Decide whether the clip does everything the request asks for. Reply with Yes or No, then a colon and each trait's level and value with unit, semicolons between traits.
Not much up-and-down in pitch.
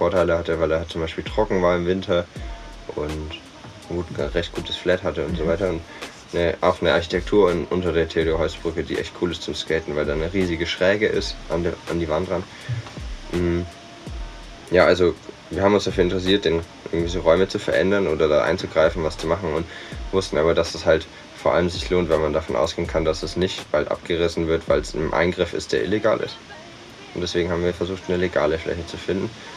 Yes: narrow, 2.3 semitones